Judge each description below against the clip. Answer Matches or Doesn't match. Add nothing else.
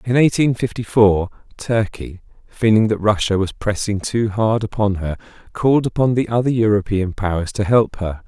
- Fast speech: Doesn't match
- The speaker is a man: Matches